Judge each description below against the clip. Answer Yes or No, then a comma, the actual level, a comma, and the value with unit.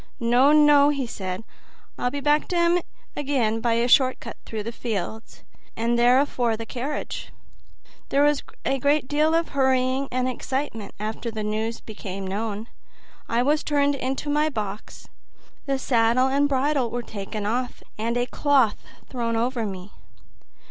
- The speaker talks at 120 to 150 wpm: No, average, 165 wpm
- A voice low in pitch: No, very high, 250 Hz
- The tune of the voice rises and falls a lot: No, average, 3.9 semitones